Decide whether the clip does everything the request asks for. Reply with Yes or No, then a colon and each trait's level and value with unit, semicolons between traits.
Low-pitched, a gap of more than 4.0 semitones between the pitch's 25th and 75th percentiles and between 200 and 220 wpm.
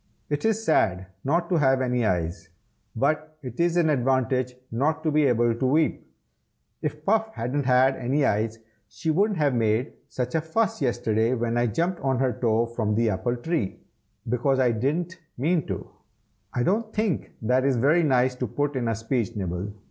No: low, 130 Hz; average, 4.9 semitones; average, 185 wpm